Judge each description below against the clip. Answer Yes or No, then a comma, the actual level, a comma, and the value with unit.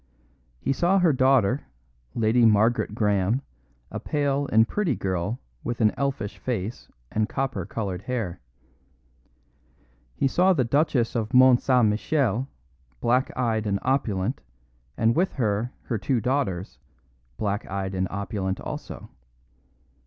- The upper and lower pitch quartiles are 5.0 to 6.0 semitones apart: No, average, 4.4 semitones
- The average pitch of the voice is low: Yes, low, 115 Hz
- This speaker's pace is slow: Yes, slow, 130 wpm